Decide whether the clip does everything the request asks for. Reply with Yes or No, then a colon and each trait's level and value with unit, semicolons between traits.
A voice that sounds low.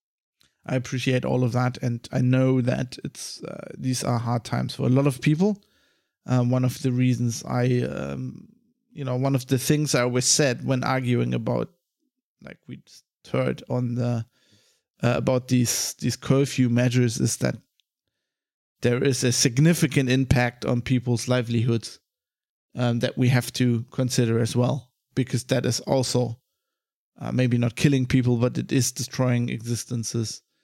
Yes: low, 125 Hz